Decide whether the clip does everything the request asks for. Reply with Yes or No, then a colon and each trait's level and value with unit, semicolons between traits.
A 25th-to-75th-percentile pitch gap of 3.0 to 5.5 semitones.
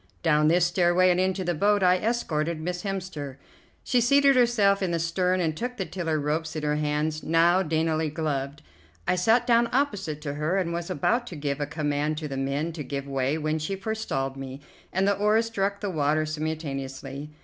Yes: average, 4.4 semitones